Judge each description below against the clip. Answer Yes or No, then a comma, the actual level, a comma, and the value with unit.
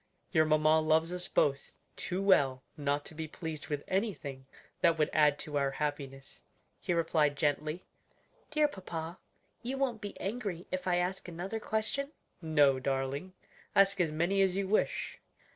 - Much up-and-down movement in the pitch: No, average, 4.6 semitones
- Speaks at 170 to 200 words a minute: No, average, 160 wpm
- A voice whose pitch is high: No, medium, 160 Hz